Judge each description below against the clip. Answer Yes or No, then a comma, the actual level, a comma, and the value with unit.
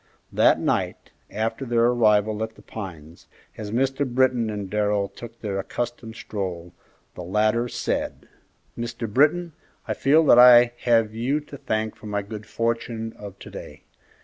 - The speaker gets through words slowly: No, average, 155 wpm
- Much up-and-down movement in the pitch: No, narrow, 2.6 semitones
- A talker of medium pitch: No, low, 115 Hz